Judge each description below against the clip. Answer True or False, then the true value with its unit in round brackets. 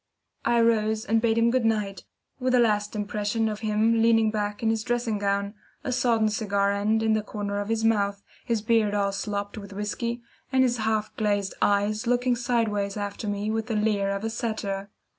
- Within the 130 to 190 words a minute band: False (200 wpm)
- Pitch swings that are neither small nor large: False (1.9 semitones)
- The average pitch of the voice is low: False (215 Hz)